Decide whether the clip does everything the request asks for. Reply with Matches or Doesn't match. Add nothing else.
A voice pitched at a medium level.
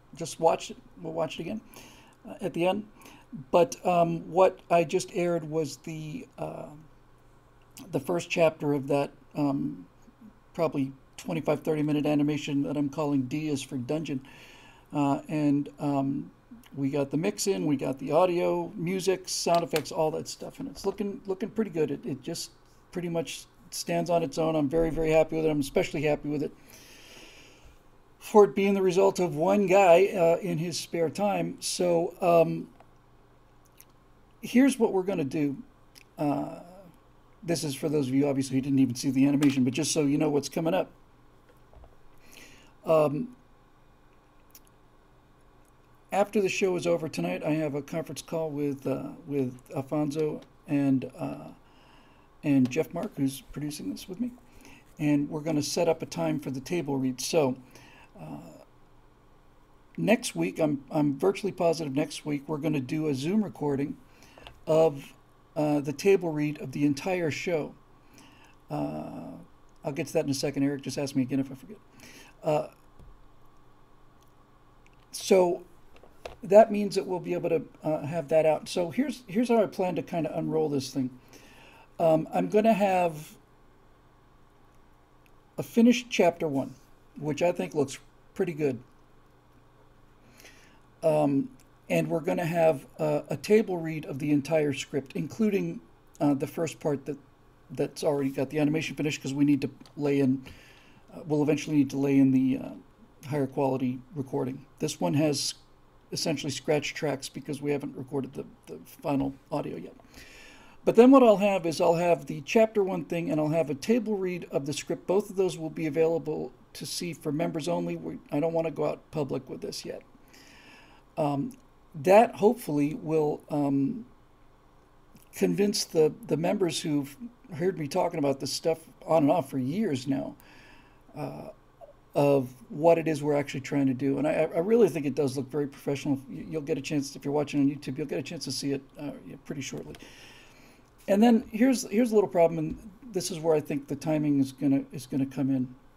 Matches